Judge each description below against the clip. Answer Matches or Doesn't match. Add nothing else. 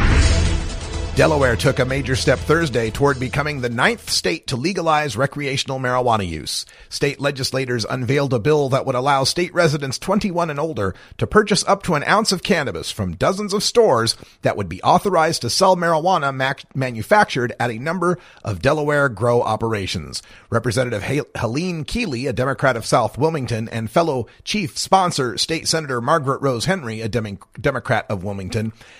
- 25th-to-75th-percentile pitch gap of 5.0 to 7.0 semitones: Matches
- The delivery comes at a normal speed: Matches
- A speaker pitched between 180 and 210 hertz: Doesn't match